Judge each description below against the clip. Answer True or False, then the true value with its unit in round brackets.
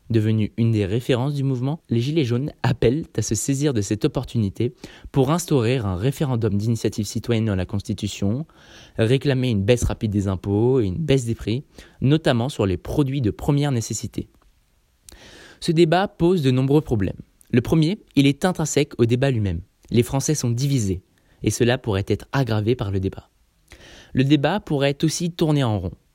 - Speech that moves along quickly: False (175 wpm)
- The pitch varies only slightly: False (5.0 semitones)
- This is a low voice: True (125 Hz)